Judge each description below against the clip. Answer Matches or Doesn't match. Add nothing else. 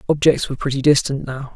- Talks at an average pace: Matches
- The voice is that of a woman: Doesn't match